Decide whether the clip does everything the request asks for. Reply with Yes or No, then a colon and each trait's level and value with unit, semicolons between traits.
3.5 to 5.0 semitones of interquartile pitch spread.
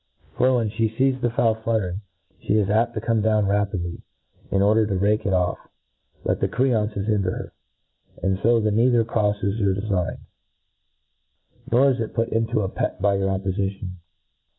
No: average, 2.7 semitones